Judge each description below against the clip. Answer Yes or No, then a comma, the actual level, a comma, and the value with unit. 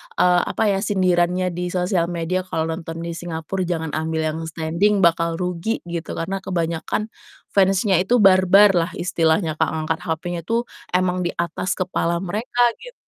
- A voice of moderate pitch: Yes, medium, 180 Hz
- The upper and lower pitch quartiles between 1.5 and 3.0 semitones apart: Yes, narrow, 2.4 semitones